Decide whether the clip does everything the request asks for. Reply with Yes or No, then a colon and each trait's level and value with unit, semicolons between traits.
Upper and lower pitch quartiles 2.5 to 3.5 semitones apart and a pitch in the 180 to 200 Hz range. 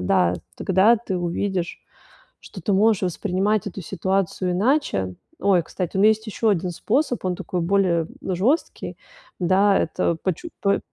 Yes: average, 2.8 semitones; high, 190 Hz